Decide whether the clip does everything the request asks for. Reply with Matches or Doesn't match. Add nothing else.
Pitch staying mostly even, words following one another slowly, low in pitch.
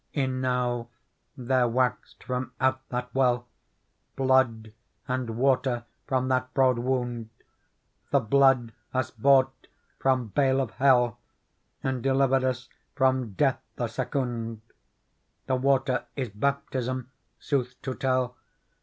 Matches